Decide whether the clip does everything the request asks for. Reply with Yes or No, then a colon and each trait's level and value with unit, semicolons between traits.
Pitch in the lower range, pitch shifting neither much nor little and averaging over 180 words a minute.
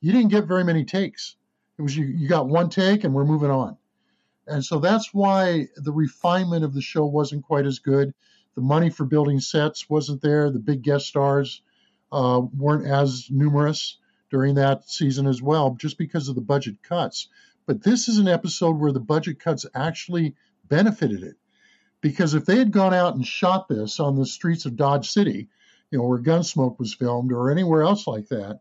No: medium, 150 Hz; average, 3.9 semitones; average, 195 wpm